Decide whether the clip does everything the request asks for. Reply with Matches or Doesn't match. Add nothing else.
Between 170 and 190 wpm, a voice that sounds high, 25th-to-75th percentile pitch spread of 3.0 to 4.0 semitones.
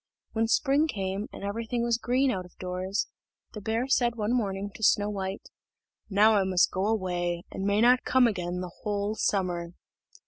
Matches